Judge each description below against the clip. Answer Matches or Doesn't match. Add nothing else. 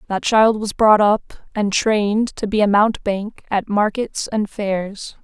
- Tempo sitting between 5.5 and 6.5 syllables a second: Doesn't match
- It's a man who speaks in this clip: Doesn't match